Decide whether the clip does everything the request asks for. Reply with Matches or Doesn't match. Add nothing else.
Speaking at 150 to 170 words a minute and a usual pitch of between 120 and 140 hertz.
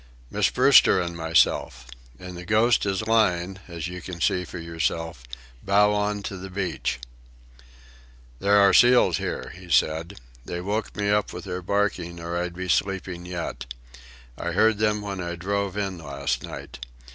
Doesn't match